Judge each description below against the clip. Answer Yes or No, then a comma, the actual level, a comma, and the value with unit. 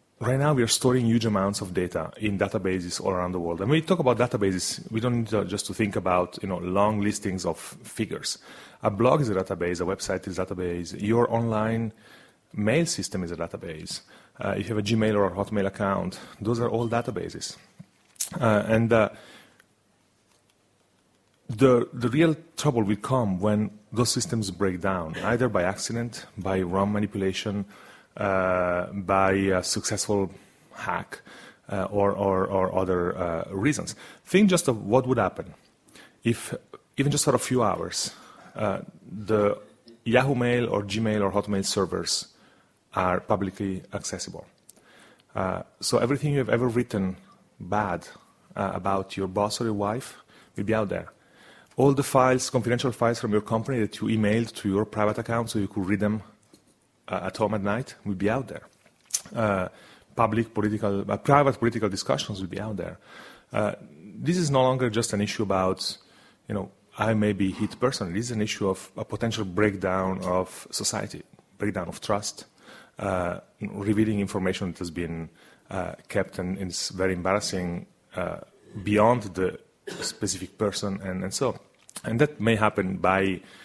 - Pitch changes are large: No, average, 3.3 semitones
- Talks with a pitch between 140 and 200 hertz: No, low, 105 Hz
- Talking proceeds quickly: No, average, 170 wpm